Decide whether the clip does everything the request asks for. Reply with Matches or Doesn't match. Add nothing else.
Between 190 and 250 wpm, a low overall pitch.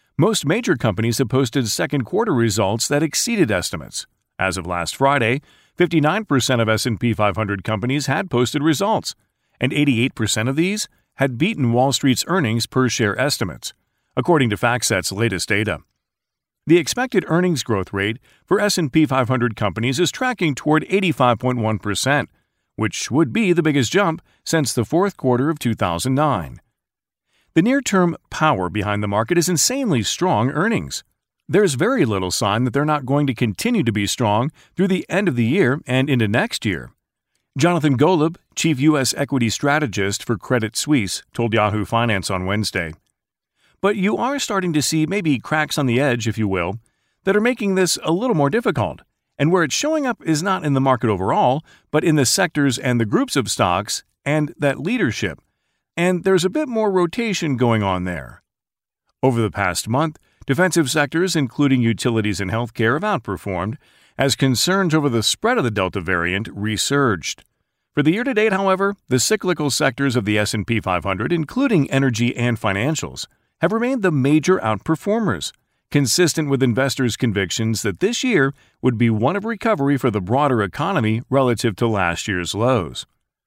Doesn't match